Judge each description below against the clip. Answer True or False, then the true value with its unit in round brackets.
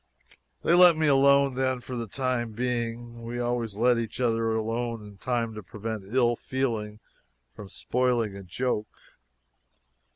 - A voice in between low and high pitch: False (120 Hz)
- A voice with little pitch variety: True (2.3 semitones)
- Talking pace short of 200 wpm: True (150 wpm)